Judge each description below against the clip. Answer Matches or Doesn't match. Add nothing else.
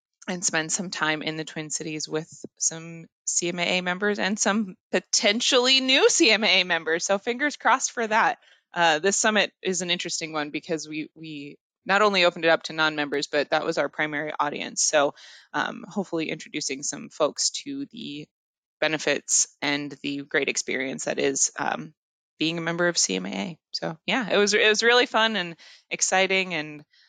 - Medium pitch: Matches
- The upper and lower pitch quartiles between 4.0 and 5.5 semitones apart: Matches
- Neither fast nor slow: Matches